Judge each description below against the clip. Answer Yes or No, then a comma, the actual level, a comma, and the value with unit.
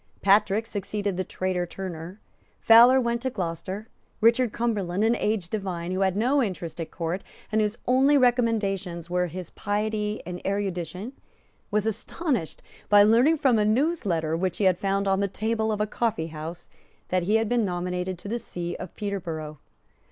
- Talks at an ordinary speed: Yes, average, 165 wpm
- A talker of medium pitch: No, high, 200 Hz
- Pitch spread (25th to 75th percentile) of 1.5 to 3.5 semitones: No, average, 3.9 semitones